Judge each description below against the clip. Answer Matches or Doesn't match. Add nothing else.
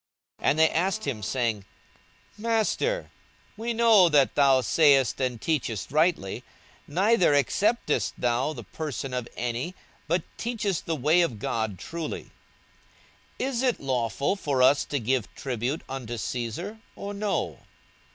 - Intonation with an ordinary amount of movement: Doesn't match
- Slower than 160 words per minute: Matches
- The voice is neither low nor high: Matches